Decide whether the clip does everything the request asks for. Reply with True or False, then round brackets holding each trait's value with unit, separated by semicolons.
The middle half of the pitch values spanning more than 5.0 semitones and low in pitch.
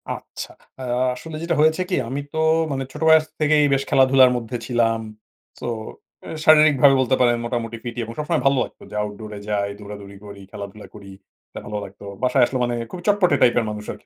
True (5.5 semitones; 125 Hz)